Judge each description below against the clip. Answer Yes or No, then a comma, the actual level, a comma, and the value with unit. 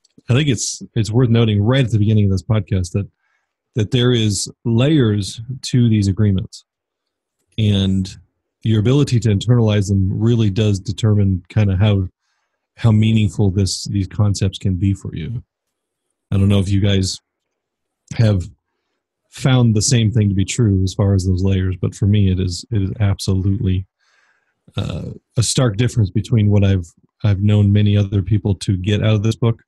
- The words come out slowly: No, average, 175 wpm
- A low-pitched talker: Yes, low, 105 Hz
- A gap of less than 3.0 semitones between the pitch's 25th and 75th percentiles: Yes, narrow, 2.5 semitones